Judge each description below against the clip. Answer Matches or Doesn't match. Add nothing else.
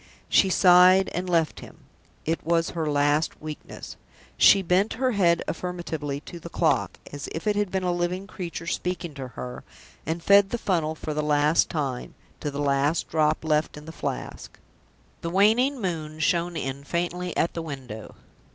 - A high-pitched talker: Doesn't match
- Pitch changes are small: Doesn't match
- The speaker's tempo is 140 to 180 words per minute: Matches